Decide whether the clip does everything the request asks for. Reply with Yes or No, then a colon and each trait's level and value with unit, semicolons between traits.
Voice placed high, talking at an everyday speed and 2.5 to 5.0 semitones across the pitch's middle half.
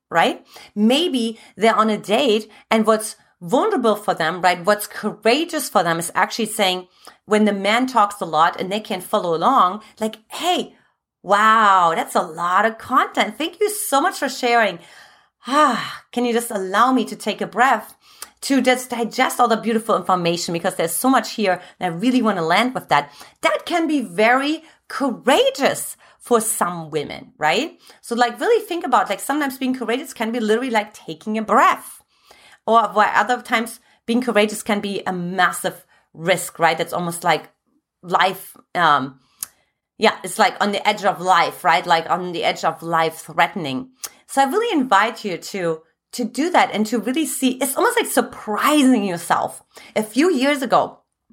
No: high, 220 Hz; average, 180 wpm; wide, 5.4 semitones